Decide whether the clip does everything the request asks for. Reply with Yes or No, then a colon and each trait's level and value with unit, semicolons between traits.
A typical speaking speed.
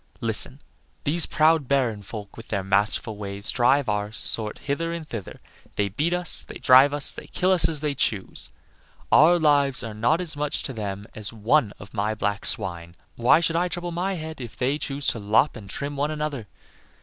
Yes: average, 195 wpm